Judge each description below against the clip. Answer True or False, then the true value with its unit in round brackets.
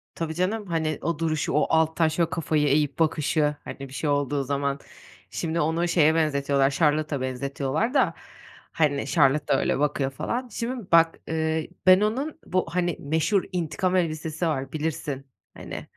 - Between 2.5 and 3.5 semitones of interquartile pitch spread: True (2.9 semitones)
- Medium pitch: True (155 Hz)